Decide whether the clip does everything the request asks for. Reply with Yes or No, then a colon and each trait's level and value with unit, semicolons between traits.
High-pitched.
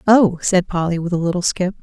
No: medium, 180 Hz